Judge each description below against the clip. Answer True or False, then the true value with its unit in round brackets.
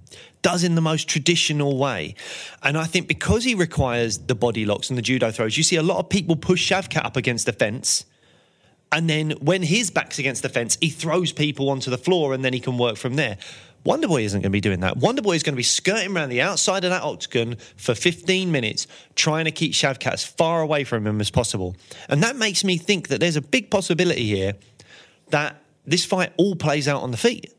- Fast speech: True (230 wpm)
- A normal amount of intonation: False (5.8 semitones)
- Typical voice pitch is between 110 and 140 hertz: False (150 Hz)